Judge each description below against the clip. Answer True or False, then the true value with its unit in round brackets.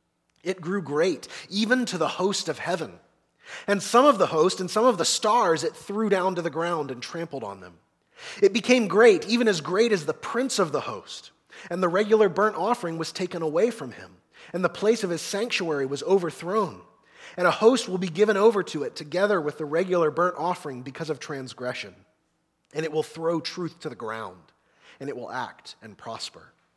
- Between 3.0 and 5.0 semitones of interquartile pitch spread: True (4.7 semitones)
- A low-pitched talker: False (175 Hz)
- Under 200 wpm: False (205 wpm)